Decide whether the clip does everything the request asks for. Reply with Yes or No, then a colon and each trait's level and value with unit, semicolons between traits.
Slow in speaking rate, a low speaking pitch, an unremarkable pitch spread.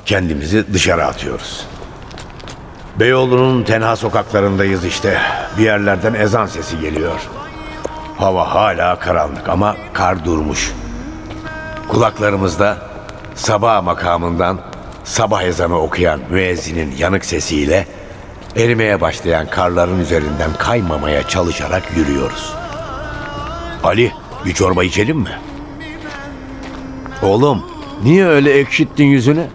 Yes: slow, 90 wpm; low, 100 Hz; average, 3.9 semitones